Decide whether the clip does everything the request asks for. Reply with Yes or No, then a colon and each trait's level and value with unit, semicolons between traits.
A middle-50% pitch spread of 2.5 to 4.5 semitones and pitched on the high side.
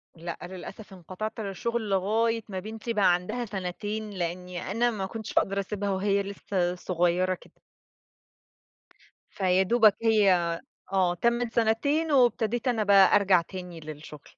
Yes: average, 3.4 semitones; high, 200 Hz